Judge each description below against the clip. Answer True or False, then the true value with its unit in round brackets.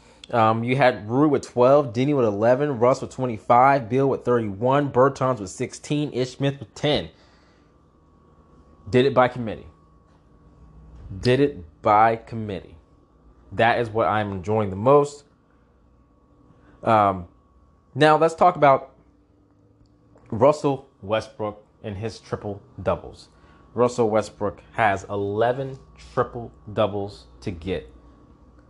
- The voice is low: True (110 Hz)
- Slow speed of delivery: True (115 wpm)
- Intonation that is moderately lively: False (6.6 semitones)